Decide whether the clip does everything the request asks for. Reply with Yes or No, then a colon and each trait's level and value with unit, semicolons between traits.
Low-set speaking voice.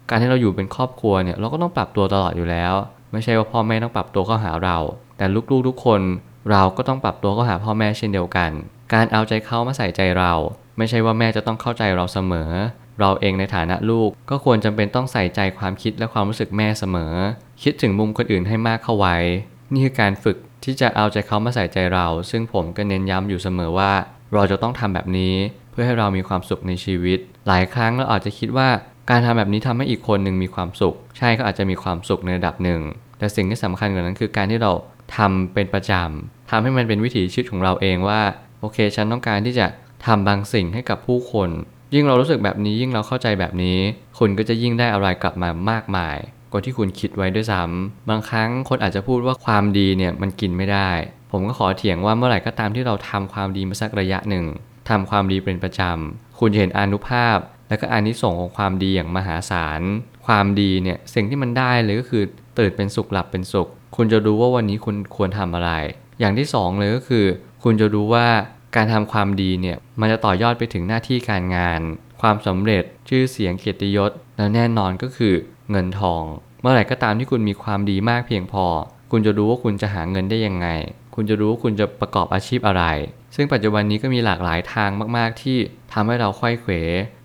Yes: low, 105 Hz